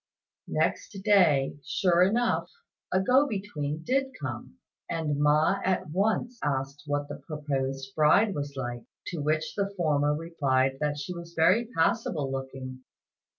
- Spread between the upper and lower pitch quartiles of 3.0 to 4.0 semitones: No, average, 5.1 semitones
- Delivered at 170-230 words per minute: No, average, 140 wpm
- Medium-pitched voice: Yes, medium, 155 Hz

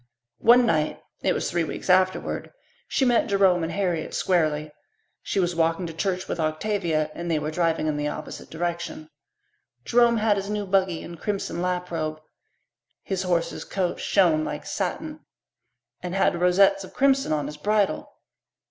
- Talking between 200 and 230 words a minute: No, average, 165 wpm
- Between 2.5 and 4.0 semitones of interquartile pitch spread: Yes, average, 3.5 semitones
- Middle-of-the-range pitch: Yes, medium, 180 Hz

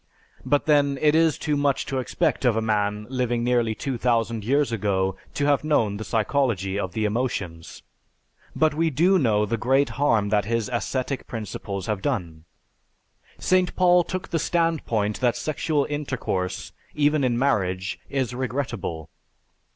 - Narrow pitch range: No, wide, 5.5 semitones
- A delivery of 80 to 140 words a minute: No, average, 155 wpm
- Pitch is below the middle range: Yes, low, 125 Hz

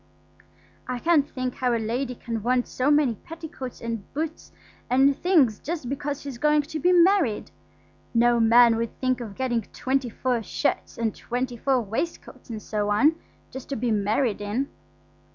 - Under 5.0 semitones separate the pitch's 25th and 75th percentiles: Yes, average, 3.6 semitones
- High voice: Yes, very high, 250 Hz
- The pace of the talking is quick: No, average, 170 wpm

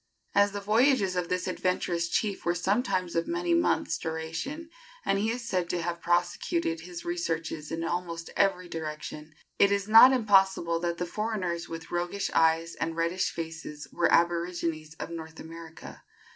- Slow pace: No, average, 160 wpm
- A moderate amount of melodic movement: Yes, average, 3.3 semitones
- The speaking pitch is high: No, medium, 175 Hz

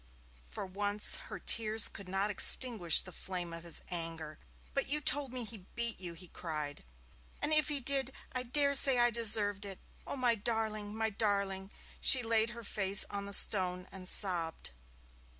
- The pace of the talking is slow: No, average, 175 wpm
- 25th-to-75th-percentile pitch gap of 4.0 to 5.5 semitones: Yes, average, 4.3 semitones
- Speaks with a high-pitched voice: Yes, high, 205 Hz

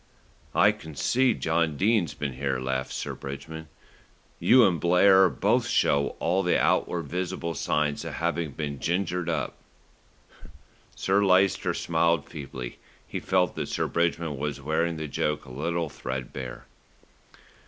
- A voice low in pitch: Yes, very low, 80 Hz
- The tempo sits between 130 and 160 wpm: Yes, average, 140 wpm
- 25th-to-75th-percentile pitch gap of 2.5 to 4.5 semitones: Yes, average, 3.9 semitones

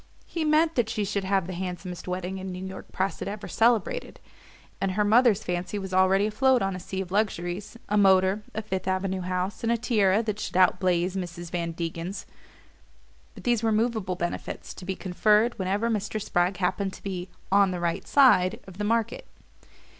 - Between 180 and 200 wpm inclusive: Yes, average, 195 wpm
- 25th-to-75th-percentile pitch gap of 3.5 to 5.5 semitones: No, average, 2.8 semitones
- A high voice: Yes, high, 195 Hz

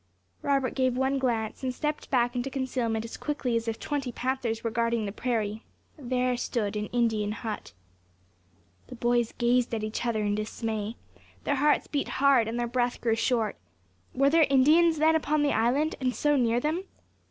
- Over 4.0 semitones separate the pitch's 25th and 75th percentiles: No, average, 3.3 semitones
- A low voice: No, high, 245 Hz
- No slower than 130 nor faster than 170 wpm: No, average, 180 wpm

